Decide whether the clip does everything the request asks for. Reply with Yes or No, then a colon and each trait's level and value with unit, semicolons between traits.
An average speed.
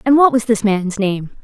No: fast, 250 wpm